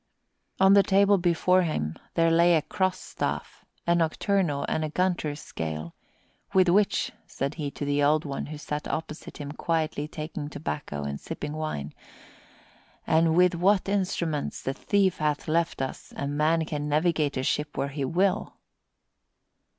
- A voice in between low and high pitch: Yes, medium, 155 Hz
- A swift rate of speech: No, average, 160 wpm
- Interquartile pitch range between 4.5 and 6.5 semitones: No, average, 3.6 semitones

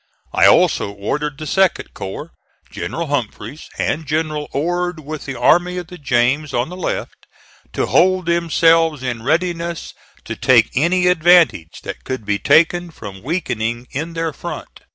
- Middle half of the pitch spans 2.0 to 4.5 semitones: No, average, 5.0 semitones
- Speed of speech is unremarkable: Yes, average, 155 wpm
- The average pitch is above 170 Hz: No, medium, 155 Hz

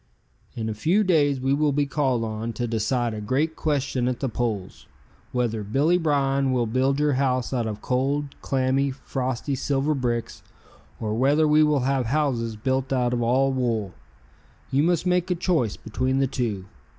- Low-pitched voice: Yes, low, 130 Hz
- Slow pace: No, average, 175 wpm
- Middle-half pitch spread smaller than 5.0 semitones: Yes, average, 3.4 semitones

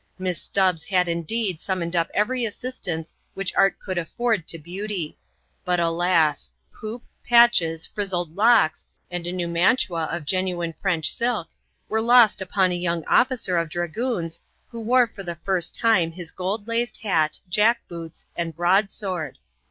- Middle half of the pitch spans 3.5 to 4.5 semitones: Yes, average, 4.2 semitones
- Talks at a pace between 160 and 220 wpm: No, average, 150 wpm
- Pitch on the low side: No, medium, 180 Hz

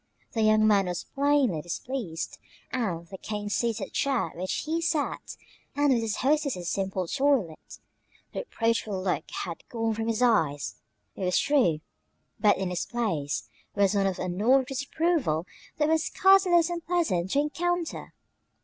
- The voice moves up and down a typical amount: No, wide, 7.7 semitones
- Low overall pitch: No, high, 225 Hz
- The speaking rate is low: No, average, 155 wpm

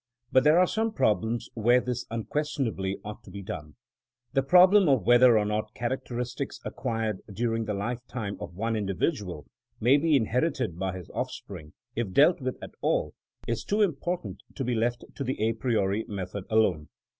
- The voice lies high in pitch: No, low, 115 Hz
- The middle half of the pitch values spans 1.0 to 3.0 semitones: No, average, 4.6 semitones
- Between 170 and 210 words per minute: Yes, average, 180 wpm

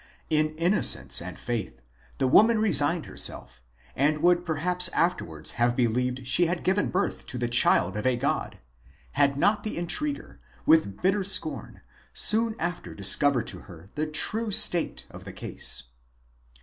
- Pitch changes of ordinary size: No, wide, 6.6 semitones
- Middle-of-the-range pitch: Yes, medium, 155 Hz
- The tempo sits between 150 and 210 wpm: Yes, average, 160 wpm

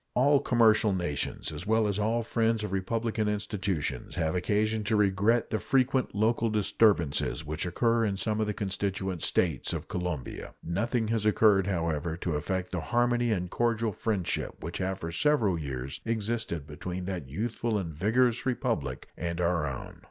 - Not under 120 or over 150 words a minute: No, average, 165 wpm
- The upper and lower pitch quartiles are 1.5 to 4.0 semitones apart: No, average, 4.7 semitones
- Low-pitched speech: Yes, low, 100 Hz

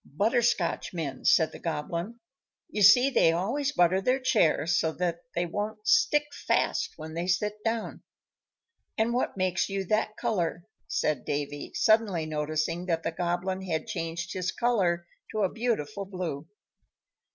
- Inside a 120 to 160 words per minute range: Yes, average, 145 wpm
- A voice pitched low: No, medium, 180 Hz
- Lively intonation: No, average, 4.7 semitones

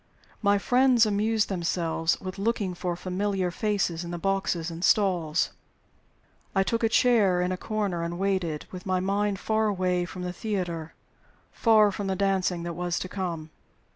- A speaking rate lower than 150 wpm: No, average, 165 wpm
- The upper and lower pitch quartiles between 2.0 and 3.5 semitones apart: Yes, average, 2.8 semitones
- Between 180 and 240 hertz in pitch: Yes, medium, 185 Hz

